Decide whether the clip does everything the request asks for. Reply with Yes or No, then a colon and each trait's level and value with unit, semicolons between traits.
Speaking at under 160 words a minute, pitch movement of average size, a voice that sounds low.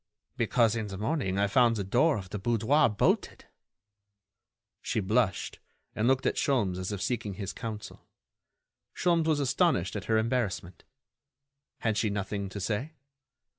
Yes: average, 150 wpm; average, 4.1 semitones; low, 110 Hz